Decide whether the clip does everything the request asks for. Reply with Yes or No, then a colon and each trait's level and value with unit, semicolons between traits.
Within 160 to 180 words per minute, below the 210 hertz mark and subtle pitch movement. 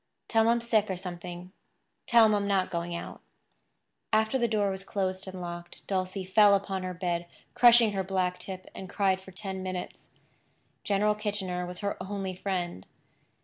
Yes: average, 175 wpm; high, 190 Hz; narrow, 2.2 semitones